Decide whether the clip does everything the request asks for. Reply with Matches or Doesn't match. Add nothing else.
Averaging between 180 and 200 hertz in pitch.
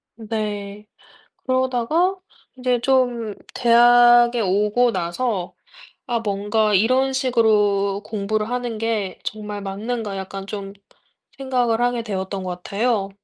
Doesn't match